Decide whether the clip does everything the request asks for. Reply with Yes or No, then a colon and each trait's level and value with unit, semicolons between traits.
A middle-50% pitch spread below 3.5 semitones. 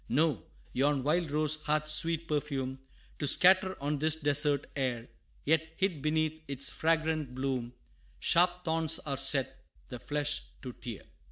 Yes: average, 2.8 semitones